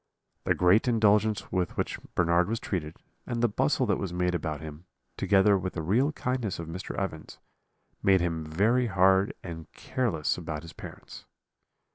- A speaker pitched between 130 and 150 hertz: No, very low, 95 Hz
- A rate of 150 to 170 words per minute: Yes, average, 165 wpm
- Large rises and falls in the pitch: No, average, 4.2 semitones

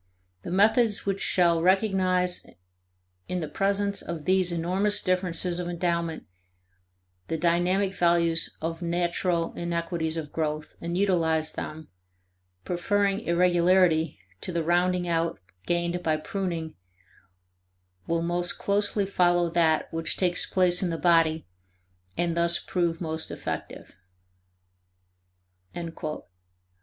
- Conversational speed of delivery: No, slow, 110 wpm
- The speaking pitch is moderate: Yes, medium, 175 Hz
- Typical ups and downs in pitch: No, narrow, 1.7 semitones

